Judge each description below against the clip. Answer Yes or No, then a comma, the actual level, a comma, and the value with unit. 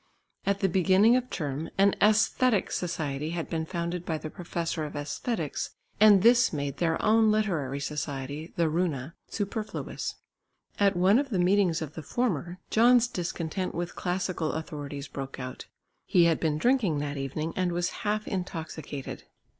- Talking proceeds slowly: No, average, 155 wpm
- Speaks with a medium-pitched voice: Yes, medium, 175 Hz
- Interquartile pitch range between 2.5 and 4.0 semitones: No, average, 4.7 semitones